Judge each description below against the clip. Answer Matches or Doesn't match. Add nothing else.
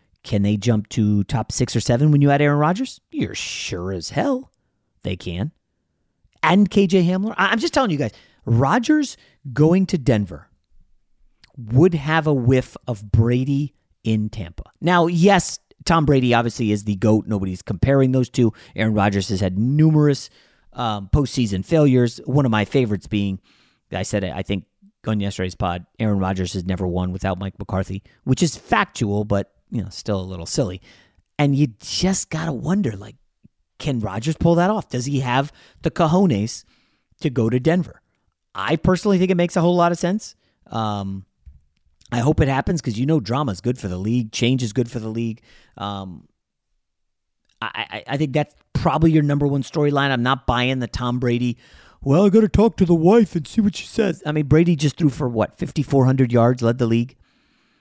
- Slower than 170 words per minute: Doesn't match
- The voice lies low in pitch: Matches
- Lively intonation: Matches